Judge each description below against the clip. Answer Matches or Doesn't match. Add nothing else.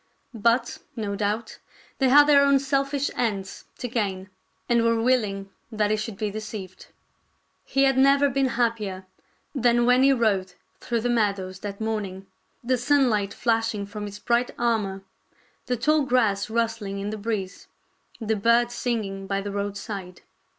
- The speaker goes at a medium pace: Matches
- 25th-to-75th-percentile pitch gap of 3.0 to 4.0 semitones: Matches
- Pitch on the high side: Matches